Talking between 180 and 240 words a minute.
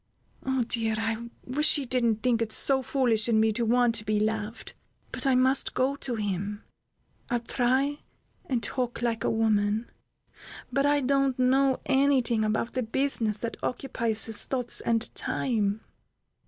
No: average, 165 wpm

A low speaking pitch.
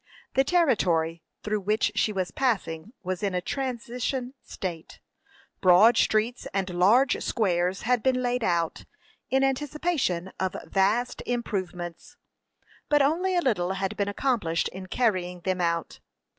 No: high, 205 Hz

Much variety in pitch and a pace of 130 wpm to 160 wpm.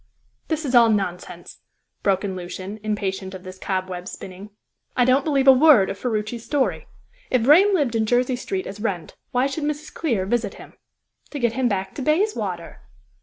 No: wide, 5.8 semitones; average, 180 wpm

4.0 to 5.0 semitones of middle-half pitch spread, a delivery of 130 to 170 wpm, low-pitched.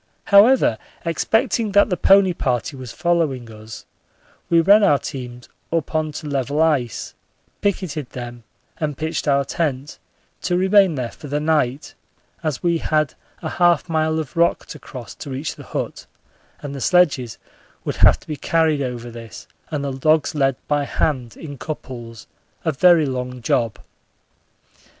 No: average, 4.6 semitones; average, 160 wpm; medium, 150 Hz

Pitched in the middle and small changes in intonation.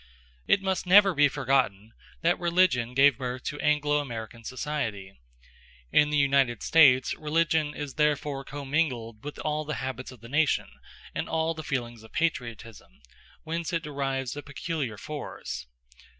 No: medium, 145 Hz; average, 3.6 semitones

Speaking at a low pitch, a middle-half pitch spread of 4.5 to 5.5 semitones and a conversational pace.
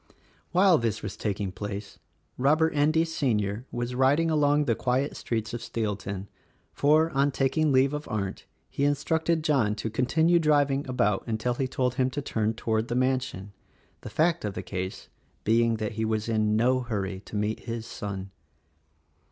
Yes: low, 120 Hz; average, 5.2 semitones; average, 170 wpm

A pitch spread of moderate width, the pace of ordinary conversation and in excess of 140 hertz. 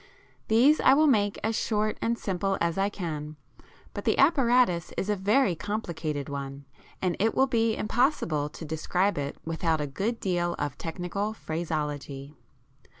No: wide, 6.0 semitones; average, 155 wpm; medium, 185 Hz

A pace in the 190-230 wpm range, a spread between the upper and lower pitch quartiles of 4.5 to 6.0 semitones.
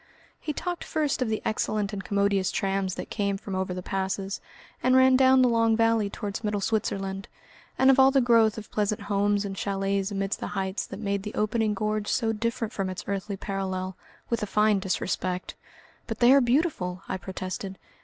No: average, 195 wpm; average, 2.8 semitones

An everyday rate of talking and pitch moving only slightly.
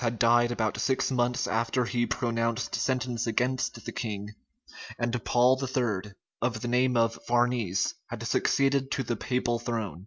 Yes: average, 155 wpm; narrow, 1.6 semitones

